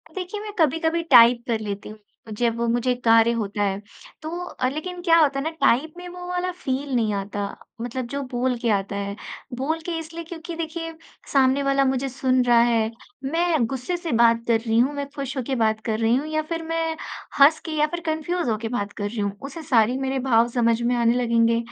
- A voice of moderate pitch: No, very high, 260 Hz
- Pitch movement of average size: No, wide, 5.7 semitones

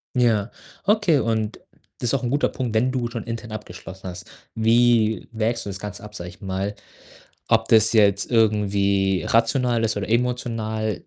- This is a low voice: Yes, low, 110 Hz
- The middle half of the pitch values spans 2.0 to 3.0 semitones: Yes, narrow, 2.6 semitones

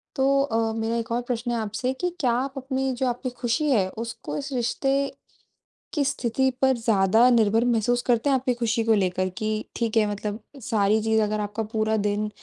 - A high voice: Yes, high, 235 Hz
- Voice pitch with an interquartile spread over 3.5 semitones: No, average, 3.1 semitones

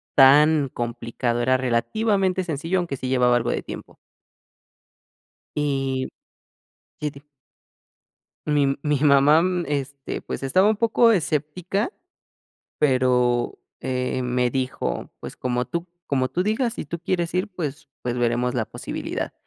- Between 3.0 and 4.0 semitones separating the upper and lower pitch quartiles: No, average, 5.1 semitones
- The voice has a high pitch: No, medium, 140 Hz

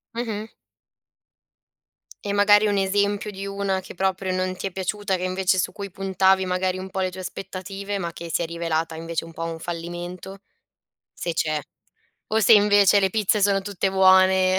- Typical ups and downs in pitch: No, narrow, 1.7 semitones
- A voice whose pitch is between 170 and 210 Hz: Yes, high, 190 Hz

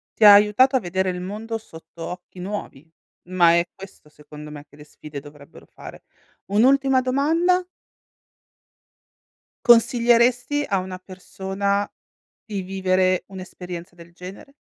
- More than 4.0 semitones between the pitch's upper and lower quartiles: Yes, average, 4.7 semitones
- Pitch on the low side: No, high, 190 Hz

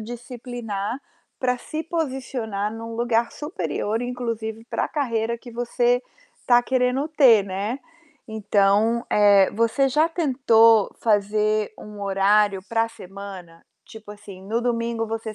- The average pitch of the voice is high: Yes, high, 225 Hz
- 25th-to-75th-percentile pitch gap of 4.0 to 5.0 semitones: No, average, 2.9 semitones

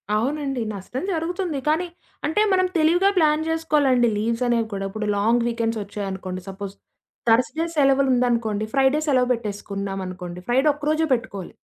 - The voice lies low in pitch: No, high, 245 Hz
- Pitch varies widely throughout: Yes, wide, 6.5 semitones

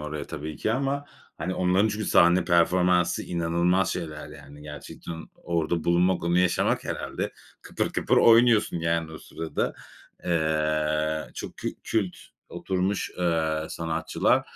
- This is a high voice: No, very low, 85 Hz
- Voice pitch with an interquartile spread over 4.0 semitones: No, average, 2.7 semitones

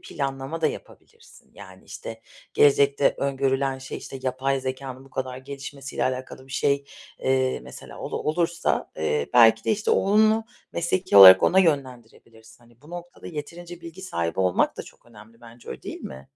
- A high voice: No, low, 135 Hz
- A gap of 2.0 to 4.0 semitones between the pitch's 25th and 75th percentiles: No, average, 4.5 semitones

